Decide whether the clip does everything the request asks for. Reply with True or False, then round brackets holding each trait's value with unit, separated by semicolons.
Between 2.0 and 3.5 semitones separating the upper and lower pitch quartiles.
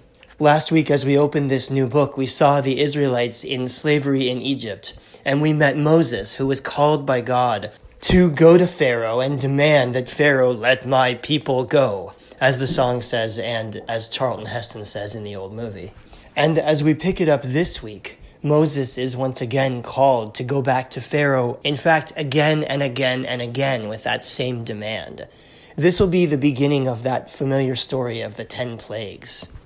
True (3.0 semitones)